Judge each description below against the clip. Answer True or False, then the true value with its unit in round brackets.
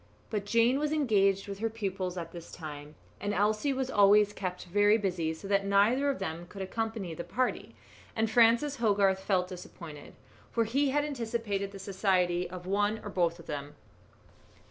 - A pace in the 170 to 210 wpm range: True (175 wpm)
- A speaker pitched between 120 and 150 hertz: False (200 Hz)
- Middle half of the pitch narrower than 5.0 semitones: True (3.8 semitones)